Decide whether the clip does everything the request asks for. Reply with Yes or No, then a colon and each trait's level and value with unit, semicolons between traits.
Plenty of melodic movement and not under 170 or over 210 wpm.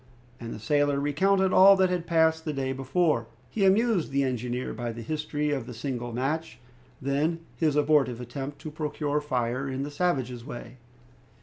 No: average, 4.2 semitones; average, 175 wpm